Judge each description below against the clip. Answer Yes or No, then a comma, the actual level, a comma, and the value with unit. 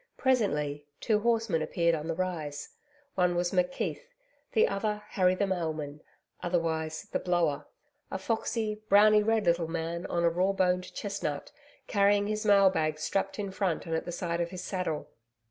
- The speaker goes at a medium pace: Yes, average, 165 wpm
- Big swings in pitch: No, average, 3.6 semitones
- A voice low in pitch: No, medium, 180 Hz